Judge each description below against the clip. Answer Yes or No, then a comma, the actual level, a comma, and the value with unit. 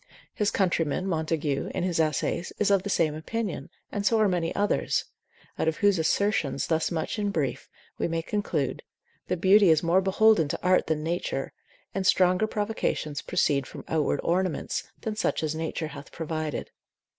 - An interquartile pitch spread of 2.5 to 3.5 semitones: No, average, 4.1 semitones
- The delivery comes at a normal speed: Yes, average, 170 wpm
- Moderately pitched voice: Yes, medium, 170 Hz